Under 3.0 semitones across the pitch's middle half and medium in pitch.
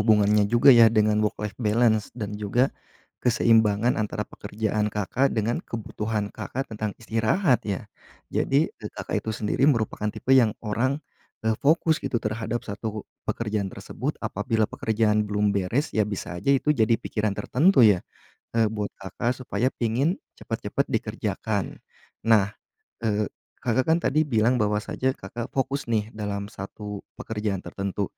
No: narrow, 2.5 semitones; low, 110 Hz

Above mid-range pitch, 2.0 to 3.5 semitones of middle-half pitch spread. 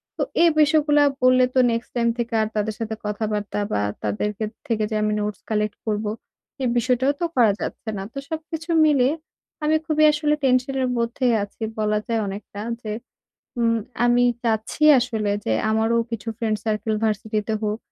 Yes: high, 230 Hz; average, 3.1 semitones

